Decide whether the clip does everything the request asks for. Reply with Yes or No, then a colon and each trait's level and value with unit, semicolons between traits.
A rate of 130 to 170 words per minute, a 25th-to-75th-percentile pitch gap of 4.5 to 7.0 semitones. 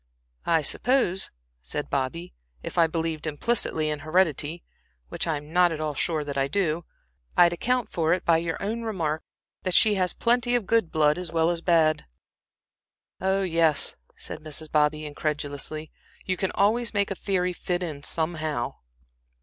No: average, 165 wpm; average, 3.3 semitones